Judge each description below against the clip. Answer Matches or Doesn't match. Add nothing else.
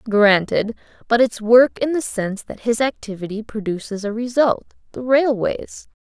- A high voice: Matches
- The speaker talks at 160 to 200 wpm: Doesn't match